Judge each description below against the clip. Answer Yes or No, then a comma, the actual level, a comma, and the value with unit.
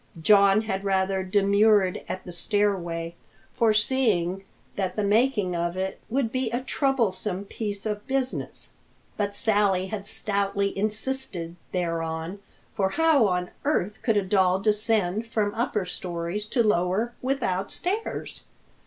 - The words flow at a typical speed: No, slow, 130 wpm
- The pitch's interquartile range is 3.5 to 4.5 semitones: No, average, 3.0 semitones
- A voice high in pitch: Yes, high, 200 Hz